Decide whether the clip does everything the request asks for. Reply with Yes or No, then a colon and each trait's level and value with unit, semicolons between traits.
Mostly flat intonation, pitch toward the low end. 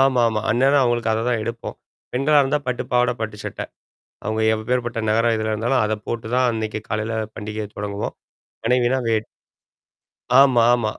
Yes: narrow, 2.3 semitones; low, 115 Hz